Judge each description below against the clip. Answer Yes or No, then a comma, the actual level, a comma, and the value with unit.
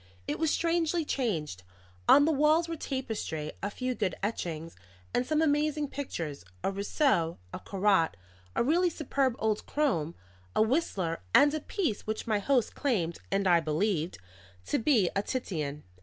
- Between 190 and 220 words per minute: No, average, 155 wpm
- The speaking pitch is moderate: No, high, 220 Hz